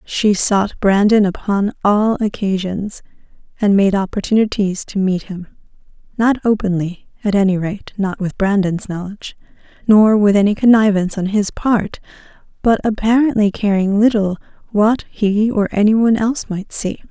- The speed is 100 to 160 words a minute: Yes, slow, 135 wpm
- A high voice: Yes, high, 205 Hz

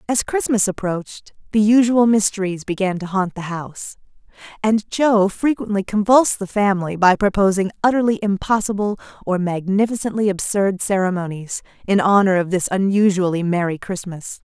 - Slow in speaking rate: Yes, slow, 130 wpm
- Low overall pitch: No, high, 200 Hz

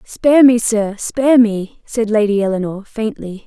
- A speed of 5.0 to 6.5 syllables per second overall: No, 4.6 syllables/s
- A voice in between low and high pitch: No, high, 220 Hz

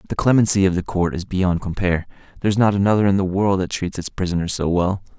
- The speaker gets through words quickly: Yes, fast, 230 wpm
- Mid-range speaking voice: No, very low, 95 Hz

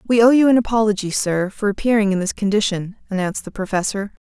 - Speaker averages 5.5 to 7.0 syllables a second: Yes, 6.4 syllables/s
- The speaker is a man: No, female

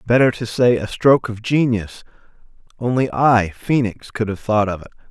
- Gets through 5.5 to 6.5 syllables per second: No, 5.0 syllables/s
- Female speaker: No, male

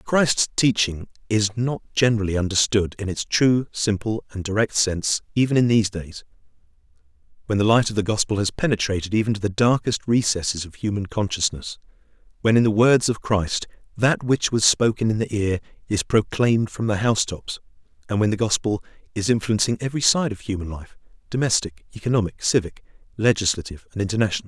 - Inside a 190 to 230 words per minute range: No, average, 165 wpm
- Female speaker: No, male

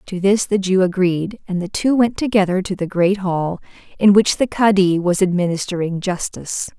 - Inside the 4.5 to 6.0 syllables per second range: Yes, 5.0 syllables/s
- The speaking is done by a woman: Yes, female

